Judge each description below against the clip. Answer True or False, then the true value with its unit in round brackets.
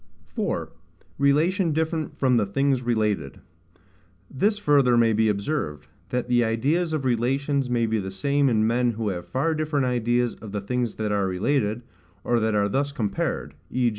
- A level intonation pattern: False (4.5 semitones)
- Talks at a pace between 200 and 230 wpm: False (170 wpm)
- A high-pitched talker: False (120 Hz)